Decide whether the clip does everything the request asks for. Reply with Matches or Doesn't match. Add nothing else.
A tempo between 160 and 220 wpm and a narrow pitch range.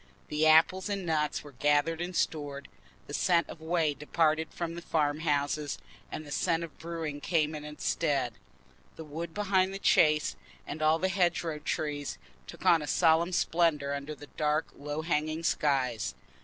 Matches